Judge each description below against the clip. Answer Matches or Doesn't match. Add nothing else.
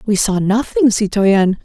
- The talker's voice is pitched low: Doesn't match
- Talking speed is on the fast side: Doesn't match